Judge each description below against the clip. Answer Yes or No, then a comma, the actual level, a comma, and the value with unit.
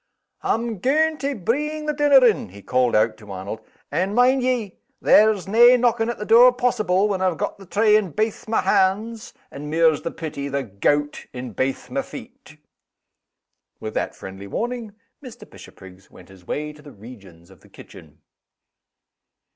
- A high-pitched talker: Yes, high, 195 Hz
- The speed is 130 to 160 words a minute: No, average, 170 wpm